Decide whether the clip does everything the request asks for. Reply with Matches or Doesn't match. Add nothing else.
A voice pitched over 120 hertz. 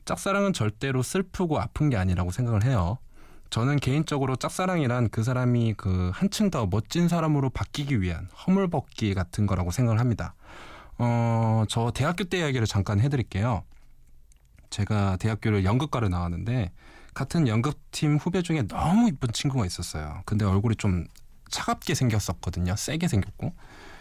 Doesn't match